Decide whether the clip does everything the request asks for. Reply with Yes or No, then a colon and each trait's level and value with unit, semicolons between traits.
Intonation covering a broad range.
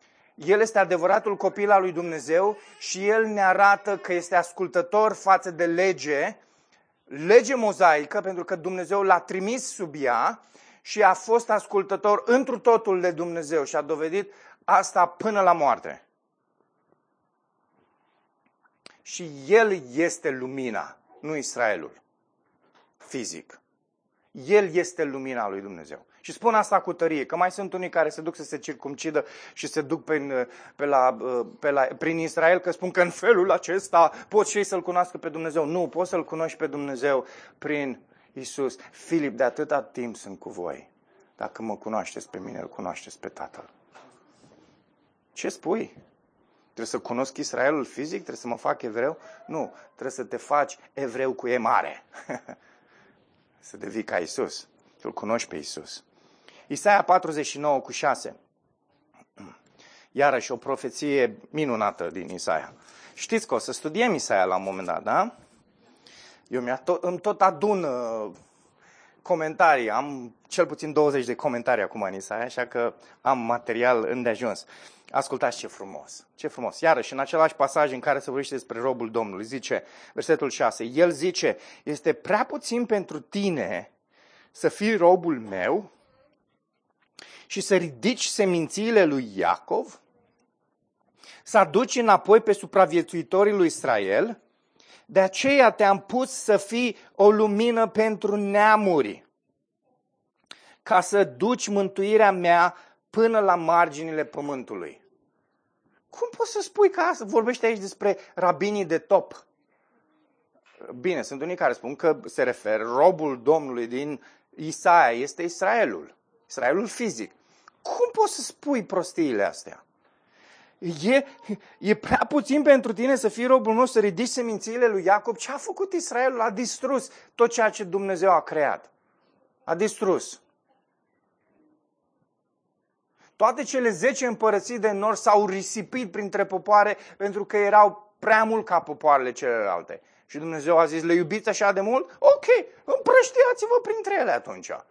Yes: wide, 5.7 semitones